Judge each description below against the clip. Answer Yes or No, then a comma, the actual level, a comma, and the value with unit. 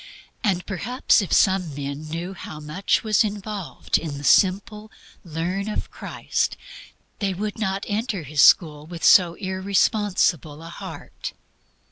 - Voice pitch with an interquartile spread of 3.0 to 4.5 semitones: Yes, average, 4.1 semitones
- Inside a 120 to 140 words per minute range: Yes, slow, 135 wpm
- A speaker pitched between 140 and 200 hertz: Yes, high, 190 Hz